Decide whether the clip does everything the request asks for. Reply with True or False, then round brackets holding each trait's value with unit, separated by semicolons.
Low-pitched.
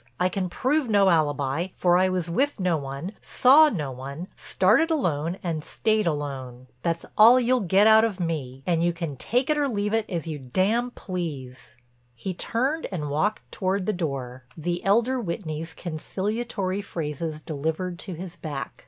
False (180 Hz)